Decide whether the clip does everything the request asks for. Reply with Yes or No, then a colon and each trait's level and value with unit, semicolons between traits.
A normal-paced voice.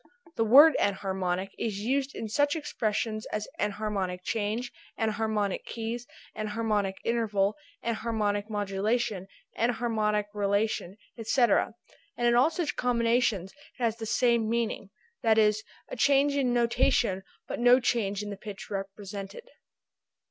No: slow, 125 wpm